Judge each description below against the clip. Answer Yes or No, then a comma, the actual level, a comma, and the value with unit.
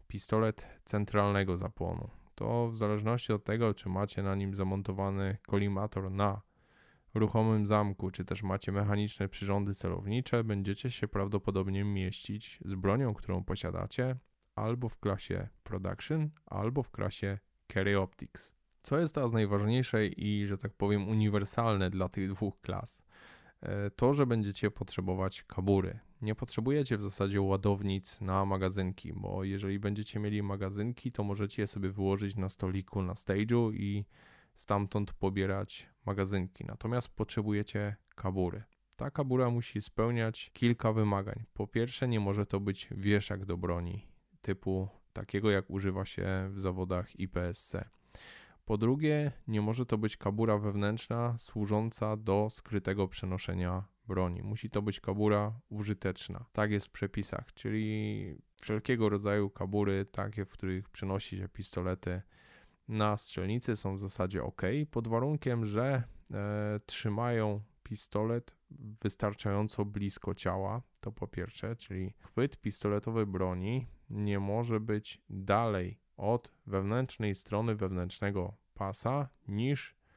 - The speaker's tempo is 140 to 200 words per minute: No, average, 130 wpm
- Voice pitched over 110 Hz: No, low, 105 Hz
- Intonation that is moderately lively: No, narrow, 2.3 semitones